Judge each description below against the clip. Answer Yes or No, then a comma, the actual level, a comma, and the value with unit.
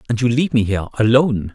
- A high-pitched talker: No, low, 120 Hz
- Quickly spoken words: Yes, fast, 235 wpm